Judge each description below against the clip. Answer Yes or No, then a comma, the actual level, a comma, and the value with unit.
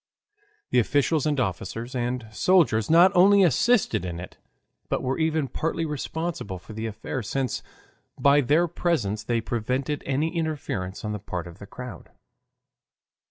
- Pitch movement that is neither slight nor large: No, wide, 6.8 semitones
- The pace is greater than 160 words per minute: No, average, 150 wpm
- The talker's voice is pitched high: No, low, 130 Hz